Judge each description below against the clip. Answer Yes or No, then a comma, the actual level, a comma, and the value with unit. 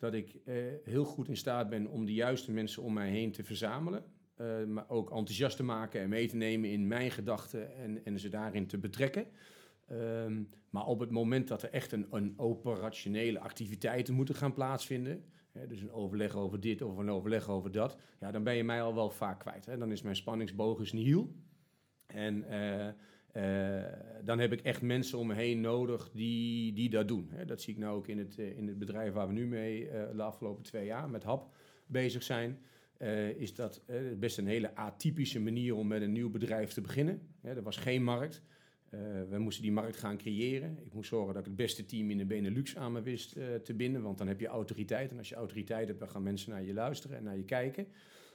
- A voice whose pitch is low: Yes, low, 110 Hz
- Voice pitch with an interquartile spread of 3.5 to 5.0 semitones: No, average, 2.7 semitones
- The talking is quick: Yes, fast, 225 wpm